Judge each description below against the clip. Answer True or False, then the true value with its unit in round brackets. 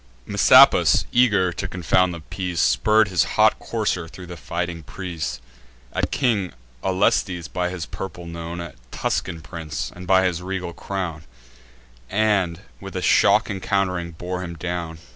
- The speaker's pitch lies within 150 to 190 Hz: False (90 Hz)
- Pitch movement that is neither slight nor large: False (2.0 semitones)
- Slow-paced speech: False (145 wpm)